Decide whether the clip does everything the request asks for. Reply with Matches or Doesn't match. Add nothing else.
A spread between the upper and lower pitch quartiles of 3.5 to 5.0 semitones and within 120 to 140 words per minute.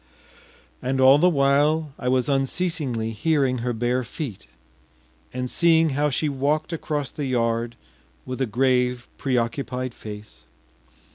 Doesn't match